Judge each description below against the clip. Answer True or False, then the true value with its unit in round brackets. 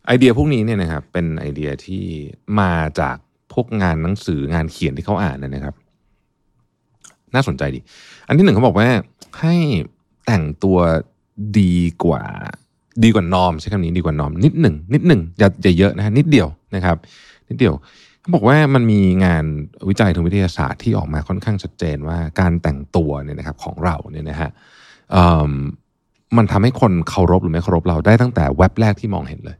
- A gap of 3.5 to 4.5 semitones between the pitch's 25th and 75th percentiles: False (5.1 semitones)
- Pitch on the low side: True (90 Hz)